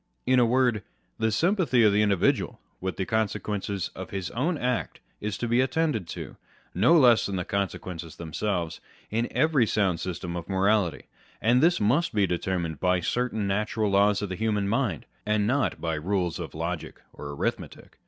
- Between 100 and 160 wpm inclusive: No, average, 180 wpm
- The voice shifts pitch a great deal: No, average, 4.5 semitones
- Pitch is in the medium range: No, low, 105 Hz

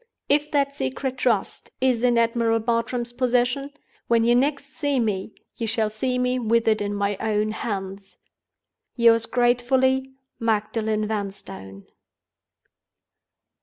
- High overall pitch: Yes, high, 230 Hz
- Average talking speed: No, slow, 120 wpm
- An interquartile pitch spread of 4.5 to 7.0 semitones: No, average, 3.0 semitones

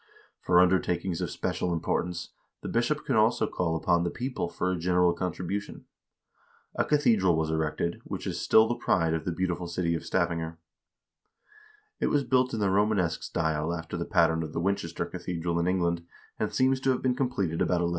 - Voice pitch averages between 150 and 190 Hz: No, very low, 90 Hz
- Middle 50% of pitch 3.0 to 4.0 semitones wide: Yes, average, 3.5 semitones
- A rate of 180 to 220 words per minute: Yes, average, 185 wpm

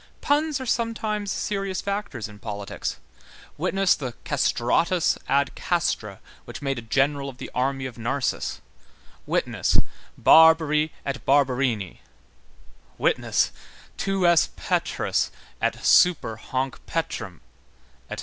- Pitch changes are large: Yes, wide, 6.8 semitones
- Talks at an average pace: No, slow, 110 wpm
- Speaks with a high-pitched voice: No, medium, 140 Hz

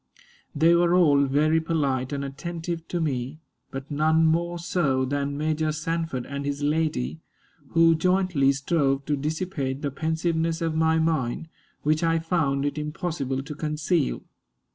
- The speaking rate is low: No, average, 145 wpm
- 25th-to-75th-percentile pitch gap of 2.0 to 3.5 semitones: Yes, average, 2.8 semitones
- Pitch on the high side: No, medium, 155 Hz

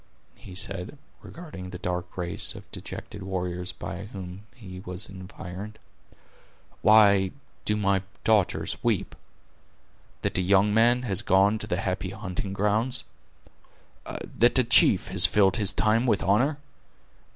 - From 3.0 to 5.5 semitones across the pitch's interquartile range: No, narrow, 2.6 semitones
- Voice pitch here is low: Yes, low, 100 Hz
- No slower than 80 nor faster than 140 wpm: Yes, slow, 135 wpm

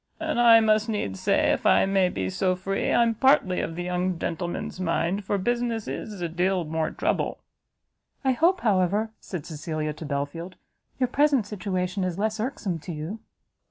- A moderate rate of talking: Yes, average, 175 wpm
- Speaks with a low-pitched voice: No, high, 190 Hz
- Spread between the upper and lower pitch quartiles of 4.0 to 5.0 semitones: Yes, average, 4.5 semitones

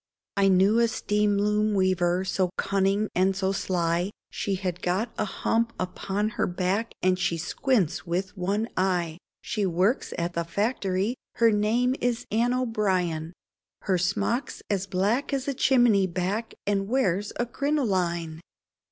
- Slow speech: No, average, 145 wpm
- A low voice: No, high, 195 Hz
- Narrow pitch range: No, average, 3.6 semitones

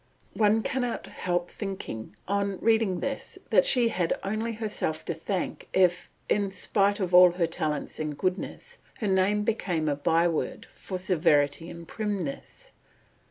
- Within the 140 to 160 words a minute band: Yes, average, 145 wpm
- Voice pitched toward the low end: No, high, 190 Hz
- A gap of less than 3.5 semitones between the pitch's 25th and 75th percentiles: No, average, 3.8 semitones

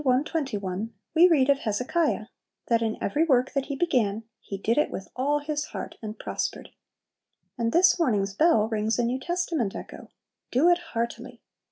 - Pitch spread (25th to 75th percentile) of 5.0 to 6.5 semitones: Yes, wide, 5.5 semitones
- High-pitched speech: Yes, very high, 255 Hz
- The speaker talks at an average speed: Yes, average, 170 wpm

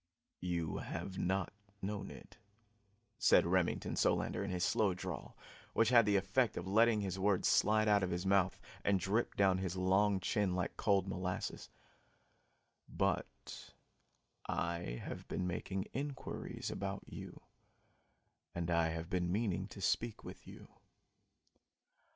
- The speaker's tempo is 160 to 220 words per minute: No, average, 140 wpm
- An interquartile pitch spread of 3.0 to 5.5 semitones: No, narrow, 2.4 semitones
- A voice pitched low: Yes, very low, 95 Hz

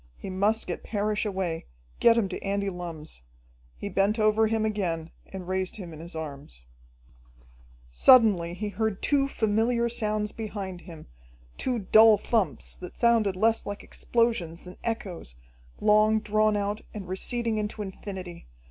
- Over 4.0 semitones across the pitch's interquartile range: No, average, 3.2 semitones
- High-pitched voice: Yes, high, 205 Hz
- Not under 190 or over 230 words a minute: No, average, 150 wpm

